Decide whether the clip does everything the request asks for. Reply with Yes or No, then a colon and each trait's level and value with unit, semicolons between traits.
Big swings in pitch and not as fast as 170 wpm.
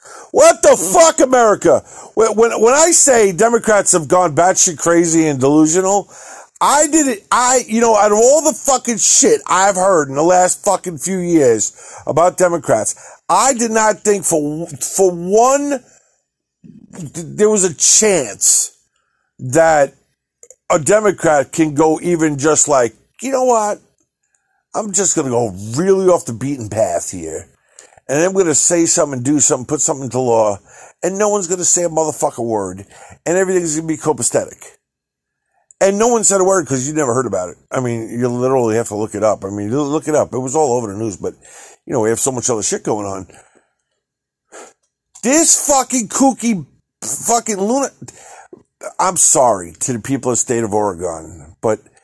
No: wide, 7.7 semitones; average, 180 wpm